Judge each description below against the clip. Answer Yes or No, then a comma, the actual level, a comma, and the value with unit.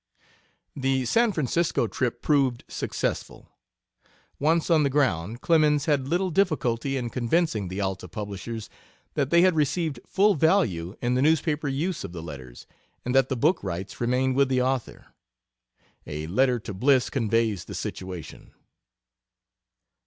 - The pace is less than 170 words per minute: Yes, average, 145 wpm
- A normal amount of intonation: No, wide, 5.8 semitones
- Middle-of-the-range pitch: No, low, 130 Hz